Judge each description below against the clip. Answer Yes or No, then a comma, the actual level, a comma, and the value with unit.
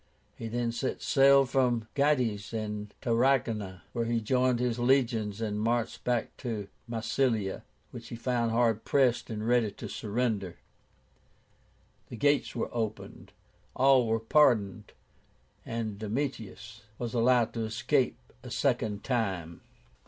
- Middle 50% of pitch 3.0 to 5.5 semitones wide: No, narrow, 2.5 semitones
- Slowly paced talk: Yes, slow, 130 wpm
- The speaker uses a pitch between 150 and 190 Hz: No, low, 115 Hz